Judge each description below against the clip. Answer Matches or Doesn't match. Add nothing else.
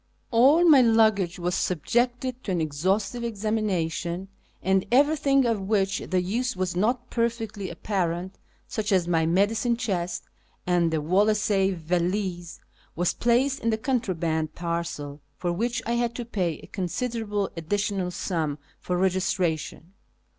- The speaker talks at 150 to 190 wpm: Doesn't match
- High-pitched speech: Matches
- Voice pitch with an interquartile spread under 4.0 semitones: Doesn't match